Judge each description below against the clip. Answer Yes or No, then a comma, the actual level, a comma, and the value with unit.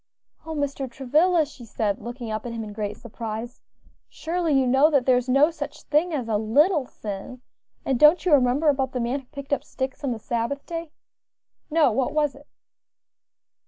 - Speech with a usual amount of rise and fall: Yes, average, 4.1 semitones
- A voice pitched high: Yes, very high, 270 Hz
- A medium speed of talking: Yes, average, 195 wpm